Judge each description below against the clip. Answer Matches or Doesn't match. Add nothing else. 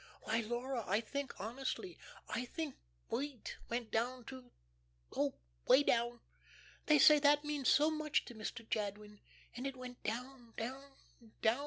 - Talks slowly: Doesn't match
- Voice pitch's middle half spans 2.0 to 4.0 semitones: Matches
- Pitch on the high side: Matches